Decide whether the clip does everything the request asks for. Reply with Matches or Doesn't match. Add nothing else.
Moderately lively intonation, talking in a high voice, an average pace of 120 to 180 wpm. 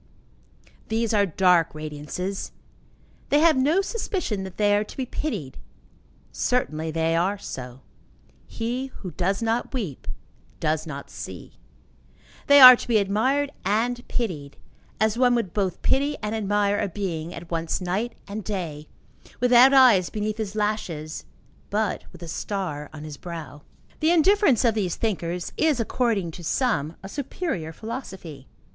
Doesn't match